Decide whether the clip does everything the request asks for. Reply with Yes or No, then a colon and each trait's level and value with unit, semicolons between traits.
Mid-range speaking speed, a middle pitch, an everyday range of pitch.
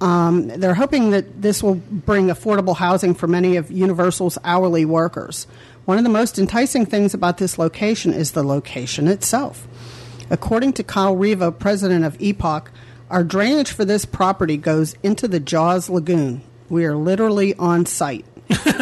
Yes: average, 160 wpm; medium, 180 Hz; average, 3.6 semitones